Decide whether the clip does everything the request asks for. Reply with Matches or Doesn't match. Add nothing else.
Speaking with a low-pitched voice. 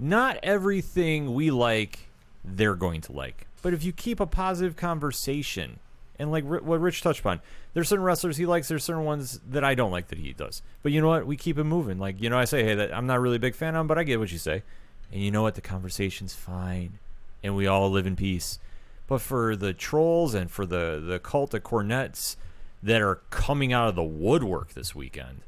Matches